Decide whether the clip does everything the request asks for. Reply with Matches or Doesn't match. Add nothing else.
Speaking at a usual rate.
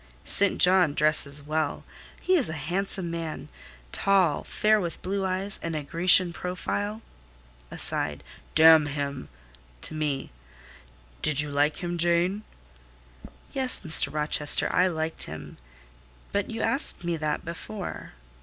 Doesn't match